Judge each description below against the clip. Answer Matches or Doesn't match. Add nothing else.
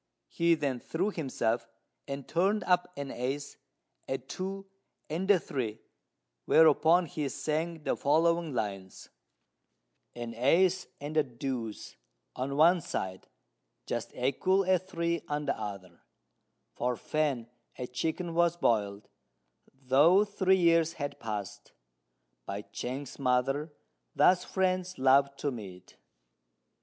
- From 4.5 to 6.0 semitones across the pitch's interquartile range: Matches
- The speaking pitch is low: Doesn't match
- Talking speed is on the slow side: Matches